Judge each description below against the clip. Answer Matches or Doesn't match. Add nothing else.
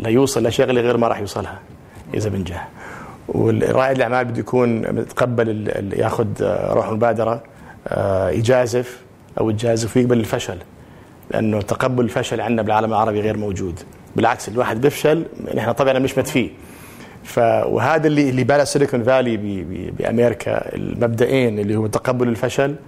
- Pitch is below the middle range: Matches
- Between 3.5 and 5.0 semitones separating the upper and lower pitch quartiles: Doesn't match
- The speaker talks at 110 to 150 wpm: Matches